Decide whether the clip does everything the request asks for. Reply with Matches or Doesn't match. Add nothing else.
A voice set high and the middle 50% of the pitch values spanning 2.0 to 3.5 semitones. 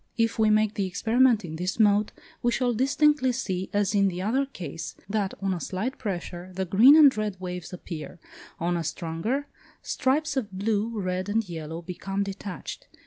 Doesn't match